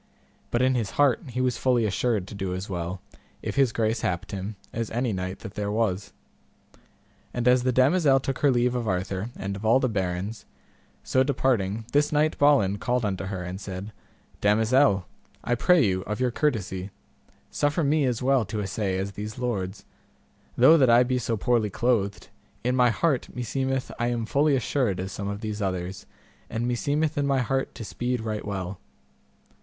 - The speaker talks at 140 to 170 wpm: No, average, 185 wpm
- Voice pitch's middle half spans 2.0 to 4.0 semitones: No, average, 4.6 semitones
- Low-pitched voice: Yes, low, 115 Hz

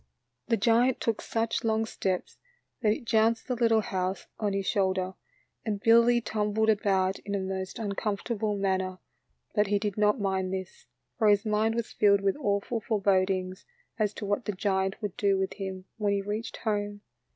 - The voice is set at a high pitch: Yes, high, 205 Hz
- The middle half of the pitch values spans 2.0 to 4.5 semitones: Yes, narrow, 2.4 semitones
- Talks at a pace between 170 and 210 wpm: Yes, average, 180 wpm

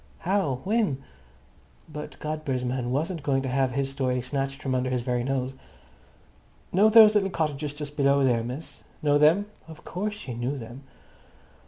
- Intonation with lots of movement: No, average, 3.6 semitones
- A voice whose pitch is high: No, medium, 140 Hz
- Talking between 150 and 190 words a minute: Yes, average, 165 wpm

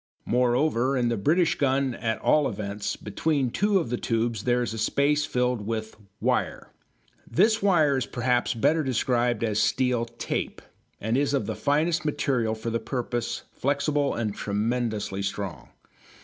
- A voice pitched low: Yes, low, 125 Hz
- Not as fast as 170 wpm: Yes, average, 155 wpm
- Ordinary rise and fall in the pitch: Yes, average, 4.0 semitones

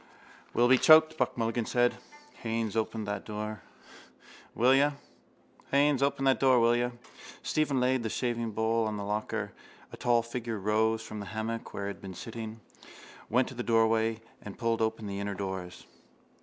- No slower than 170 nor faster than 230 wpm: No, average, 150 wpm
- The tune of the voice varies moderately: No, narrow, 2.3 semitones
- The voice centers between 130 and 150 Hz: No, low, 115 Hz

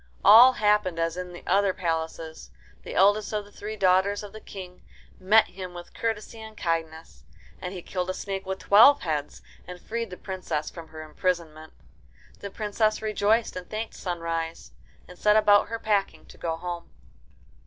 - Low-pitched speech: No, high, 190 Hz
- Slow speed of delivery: No, average, 175 wpm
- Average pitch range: Yes, average, 3.6 semitones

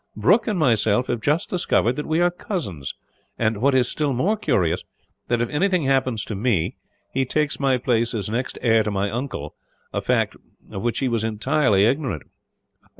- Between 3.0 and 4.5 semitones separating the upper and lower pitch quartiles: No, average, 5.1 semitones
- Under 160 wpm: No, average, 185 wpm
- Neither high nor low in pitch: No, low, 125 Hz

